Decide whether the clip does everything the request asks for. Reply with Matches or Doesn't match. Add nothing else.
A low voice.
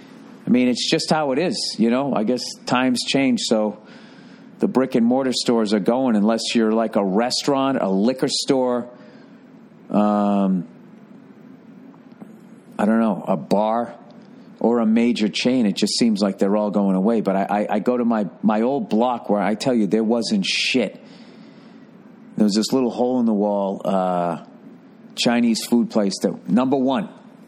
Matches